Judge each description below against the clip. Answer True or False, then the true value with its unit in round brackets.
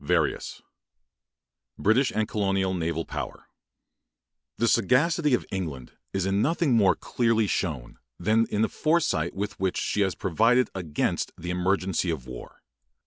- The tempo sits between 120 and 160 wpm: True (140 wpm)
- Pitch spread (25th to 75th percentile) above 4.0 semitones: True (4.7 semitones)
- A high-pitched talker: False (95 Hz)